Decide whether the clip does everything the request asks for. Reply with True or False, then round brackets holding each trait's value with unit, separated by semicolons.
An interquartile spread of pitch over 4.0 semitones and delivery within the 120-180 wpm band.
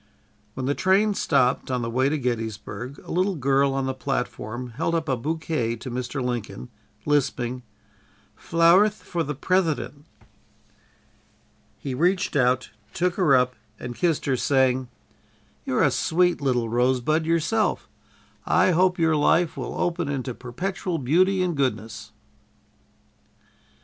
True (5.1 semitones; 140 wpm)